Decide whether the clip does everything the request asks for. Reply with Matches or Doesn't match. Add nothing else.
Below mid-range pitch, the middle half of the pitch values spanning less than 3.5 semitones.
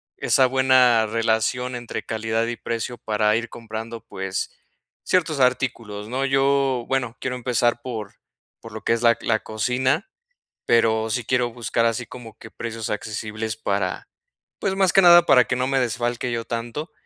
Matches